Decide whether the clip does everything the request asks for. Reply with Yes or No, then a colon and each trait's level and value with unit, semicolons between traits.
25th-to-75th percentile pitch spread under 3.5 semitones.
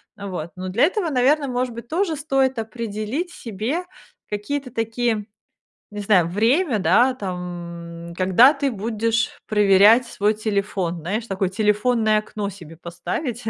No: average, 4.5 semitones